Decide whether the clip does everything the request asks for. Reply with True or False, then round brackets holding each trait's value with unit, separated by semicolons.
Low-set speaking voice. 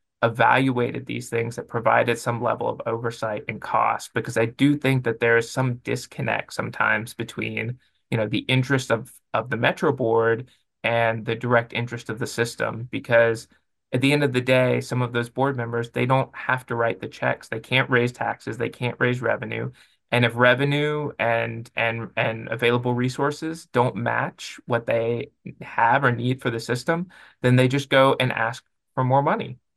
True (120 Hz)